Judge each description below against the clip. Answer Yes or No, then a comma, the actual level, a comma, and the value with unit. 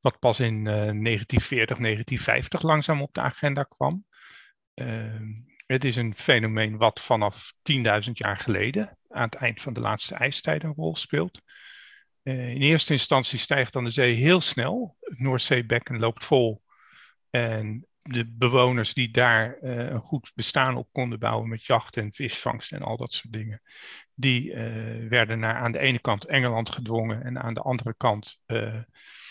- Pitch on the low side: Yes, low, 120 Hz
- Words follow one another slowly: No, average, 170 wpm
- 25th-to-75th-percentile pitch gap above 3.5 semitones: No, average, 2.8 semitones